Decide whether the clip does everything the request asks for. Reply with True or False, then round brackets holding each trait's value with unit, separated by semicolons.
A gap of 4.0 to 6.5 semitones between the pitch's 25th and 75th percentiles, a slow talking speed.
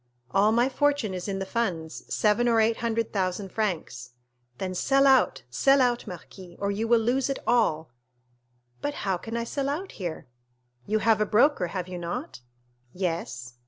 False (5.0 semitones; 175 wpm)